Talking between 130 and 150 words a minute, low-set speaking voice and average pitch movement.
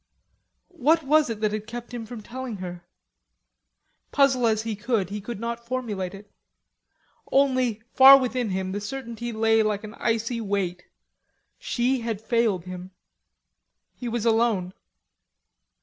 No: average, 140 wpm; high, 230 Hz; average, 3.1 semitones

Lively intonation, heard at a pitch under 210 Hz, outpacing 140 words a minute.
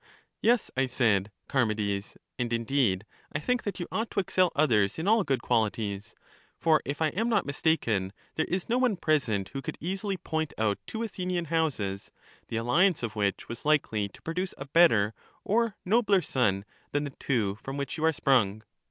Yes: wide, 8.6 semitones; medium, 140 Hz; average, 185 wpm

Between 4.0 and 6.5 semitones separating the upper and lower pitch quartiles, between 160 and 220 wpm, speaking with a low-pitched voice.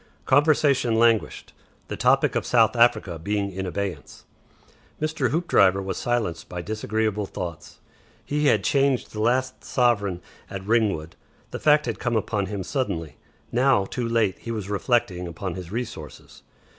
No: average, 4.3 semitones; average, 145 wpm; low, 110 Hz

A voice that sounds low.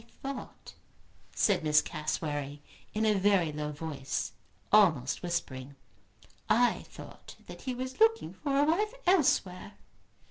No: high, 190 Hz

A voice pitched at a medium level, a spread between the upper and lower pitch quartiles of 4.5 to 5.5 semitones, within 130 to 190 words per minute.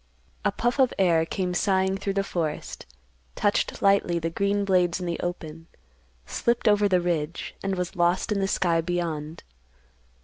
No: medium, 180 Hz; average, 2.7 semitones; average, 165 wpm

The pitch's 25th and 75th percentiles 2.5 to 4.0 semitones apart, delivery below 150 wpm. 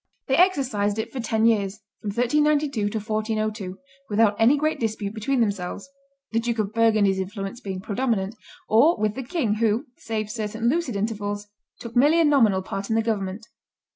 No: average, 2.9 semitones; average, 170 wpm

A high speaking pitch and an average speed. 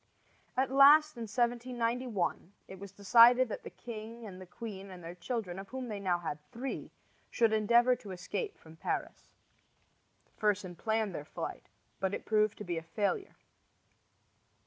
Yes: high, 215 Hz; average, 160 wpm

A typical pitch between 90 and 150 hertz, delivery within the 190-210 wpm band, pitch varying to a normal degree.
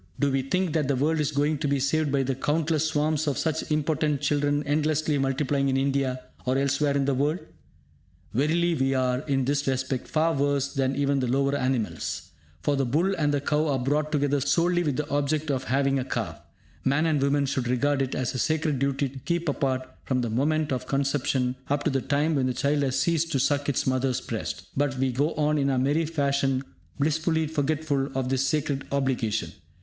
No: medium, 140 Hz; fast, 205 wpm; narrow, 2.1 semitones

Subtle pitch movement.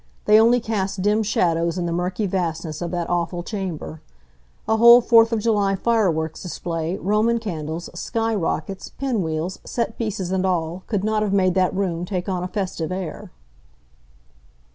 No: average, 3.8 semitones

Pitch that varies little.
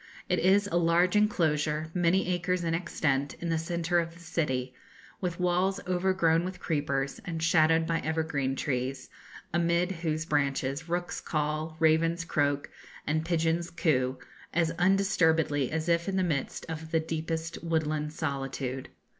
Yes: narrow, 2.3 semitones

